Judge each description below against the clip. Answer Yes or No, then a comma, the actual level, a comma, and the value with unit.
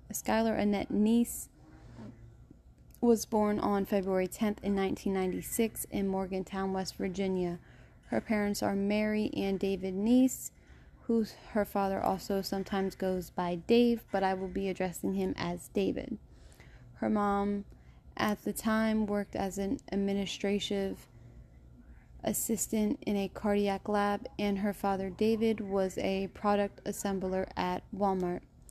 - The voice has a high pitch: Yes, high, 200 Hz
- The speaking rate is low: Yes, slow, 125 wpm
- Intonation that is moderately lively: No, narrow, 1.6 semitones